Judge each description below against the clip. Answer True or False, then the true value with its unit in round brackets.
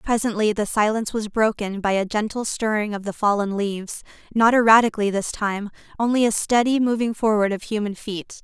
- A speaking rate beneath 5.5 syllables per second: False (5.6 syllables/s)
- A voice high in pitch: True (215 Hz)